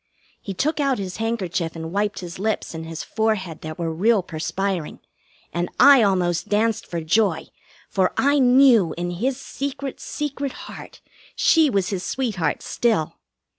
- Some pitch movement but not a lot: No, wide, 6.3 semitones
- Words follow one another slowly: No, average, 155 wpm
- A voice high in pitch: Yes, high, 200 Hz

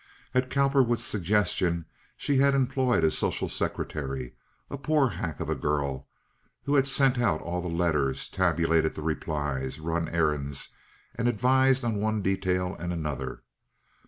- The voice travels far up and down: Yes, wide, 8.5 semitones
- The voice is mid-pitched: No, very low, 90 Hz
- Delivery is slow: No, average, 145 wpm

